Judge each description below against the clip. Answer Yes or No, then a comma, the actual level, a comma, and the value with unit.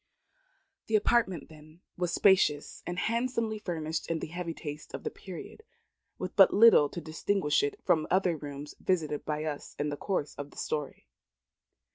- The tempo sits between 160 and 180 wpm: Yes, average, 165 wpm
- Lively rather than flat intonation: No, average, 4.5 semitones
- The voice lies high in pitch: No, medium, 165 Hz